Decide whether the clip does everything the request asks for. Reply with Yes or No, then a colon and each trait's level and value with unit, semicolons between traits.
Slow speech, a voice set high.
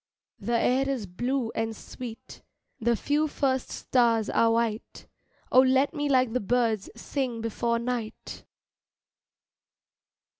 Yes: slow, 120 wpm; high, 240 Hz